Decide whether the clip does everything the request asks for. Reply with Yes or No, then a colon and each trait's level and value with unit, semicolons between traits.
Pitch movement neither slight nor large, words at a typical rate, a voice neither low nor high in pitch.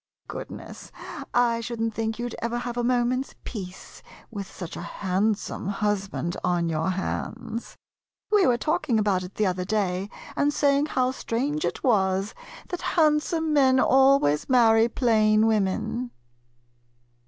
No: average, 4.7 semitones; average, 145 wpm; high, 225 Hz